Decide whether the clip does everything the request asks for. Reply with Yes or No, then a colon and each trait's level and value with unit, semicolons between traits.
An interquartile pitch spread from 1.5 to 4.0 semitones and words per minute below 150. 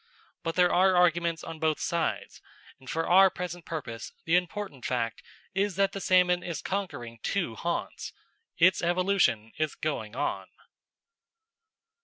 Yes: average, 3.1 semitones; average, 140 wpm